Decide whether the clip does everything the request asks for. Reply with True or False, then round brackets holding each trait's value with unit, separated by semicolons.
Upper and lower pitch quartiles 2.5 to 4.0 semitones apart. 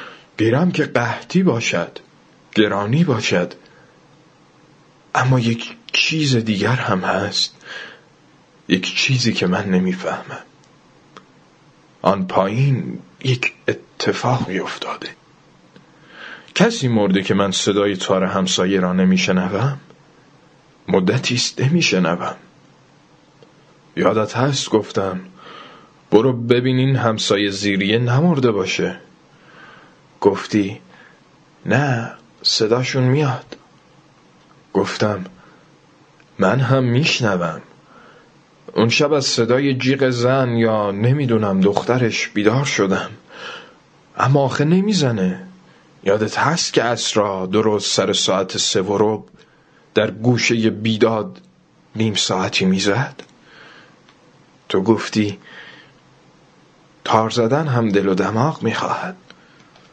False (4.9 semitones)